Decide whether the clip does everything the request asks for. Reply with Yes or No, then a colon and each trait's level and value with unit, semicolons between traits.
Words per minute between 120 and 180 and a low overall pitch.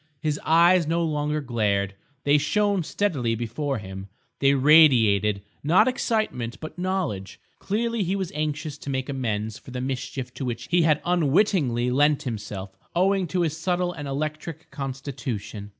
No: average, 150 wpm; medium, 145 Hz